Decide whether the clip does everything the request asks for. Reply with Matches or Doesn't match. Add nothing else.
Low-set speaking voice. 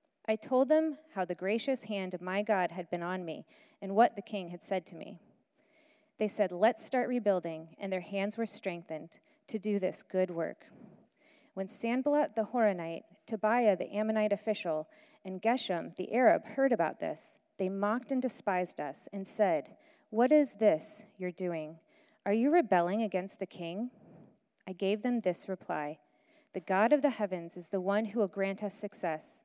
Doesn't match